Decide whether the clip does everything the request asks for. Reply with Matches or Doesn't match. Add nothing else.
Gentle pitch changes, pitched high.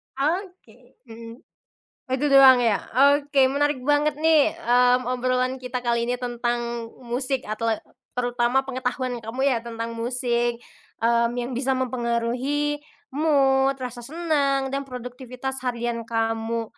Matches